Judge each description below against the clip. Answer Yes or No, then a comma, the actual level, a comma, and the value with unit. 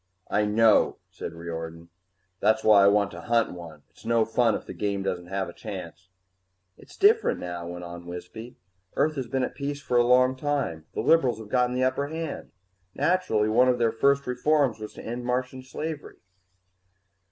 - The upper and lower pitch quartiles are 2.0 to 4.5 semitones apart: No, average, 5.2 semitones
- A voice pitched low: Yes, low, 115 Hz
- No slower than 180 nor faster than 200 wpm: Yes, average, 185 wpm